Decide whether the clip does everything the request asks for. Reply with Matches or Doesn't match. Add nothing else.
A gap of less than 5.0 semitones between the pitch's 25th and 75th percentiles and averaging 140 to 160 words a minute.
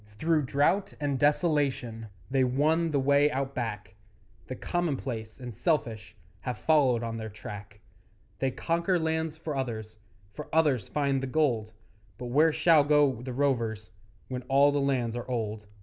Matches